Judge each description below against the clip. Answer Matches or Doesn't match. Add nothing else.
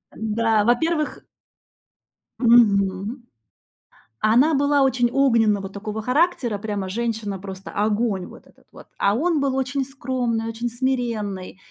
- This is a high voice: Matches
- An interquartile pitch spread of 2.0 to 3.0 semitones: Doesn't match